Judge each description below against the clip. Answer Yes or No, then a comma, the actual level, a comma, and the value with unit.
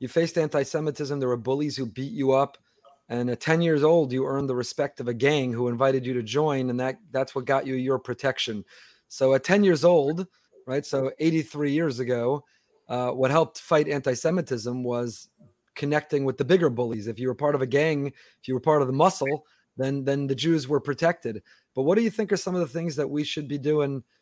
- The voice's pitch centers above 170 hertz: No, medium, 140 Hz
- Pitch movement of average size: Yes, average, 3.0 semitones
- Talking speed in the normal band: No, fast, 225 wpm